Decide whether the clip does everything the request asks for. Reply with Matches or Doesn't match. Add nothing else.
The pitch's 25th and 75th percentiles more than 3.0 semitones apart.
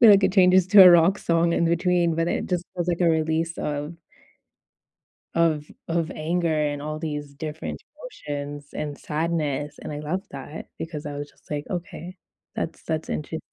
Doesn't match